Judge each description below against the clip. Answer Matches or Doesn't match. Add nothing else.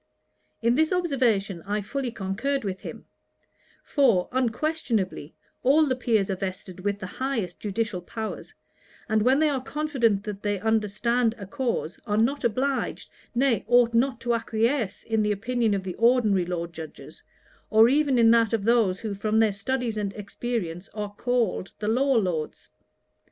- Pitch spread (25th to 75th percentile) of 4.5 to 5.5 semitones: Doesn't match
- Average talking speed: Matches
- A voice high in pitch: Matches